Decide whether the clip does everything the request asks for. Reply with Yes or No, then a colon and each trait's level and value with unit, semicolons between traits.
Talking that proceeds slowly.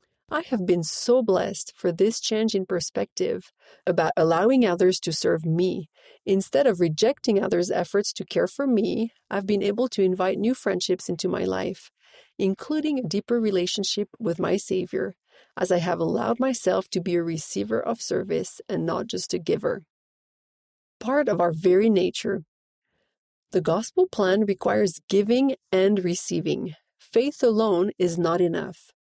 No: average, 155 wpm